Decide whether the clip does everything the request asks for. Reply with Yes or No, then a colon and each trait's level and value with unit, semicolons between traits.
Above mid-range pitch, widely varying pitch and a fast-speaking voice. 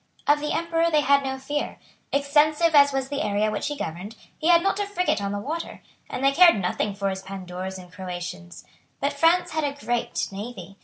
Yes: very high, 275 Hz; wide, 7.7 semitones; fast, 210 wpm